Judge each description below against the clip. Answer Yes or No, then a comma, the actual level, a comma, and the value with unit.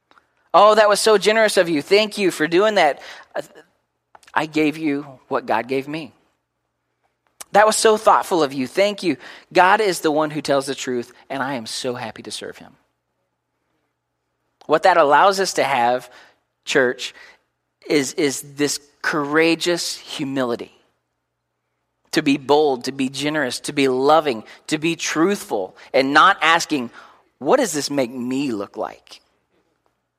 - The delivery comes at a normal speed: Yes, average, 155 wpm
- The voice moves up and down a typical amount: Yes, average, 4.9 semitones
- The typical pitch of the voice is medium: Yes, medium, 145 Hz